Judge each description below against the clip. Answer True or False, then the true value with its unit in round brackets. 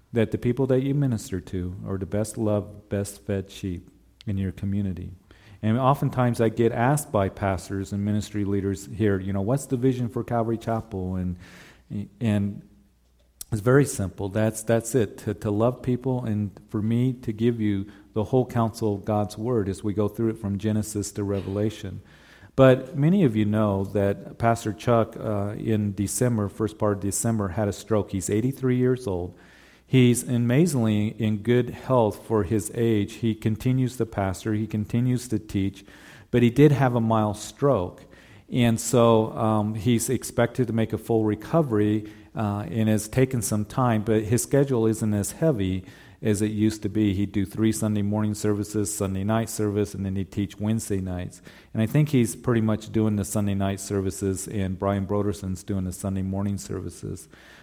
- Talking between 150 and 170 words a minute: False (180 wpm)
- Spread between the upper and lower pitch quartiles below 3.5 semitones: True (2.7 semitones)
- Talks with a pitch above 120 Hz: False (110 Hz)